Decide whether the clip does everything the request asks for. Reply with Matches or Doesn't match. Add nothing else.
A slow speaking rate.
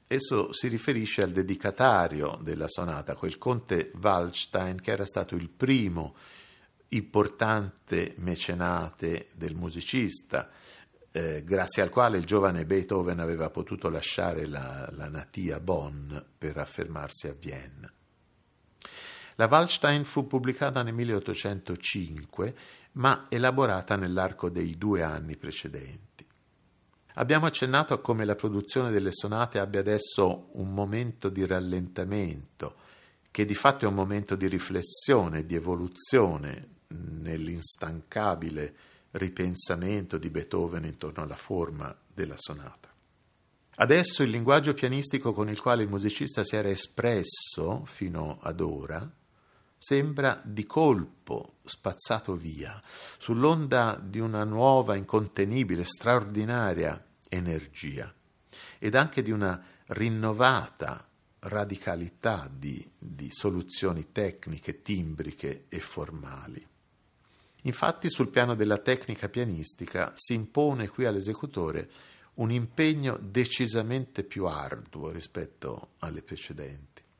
Matches